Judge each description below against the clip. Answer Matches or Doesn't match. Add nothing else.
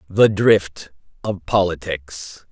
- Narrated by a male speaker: Matches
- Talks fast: Doesn't match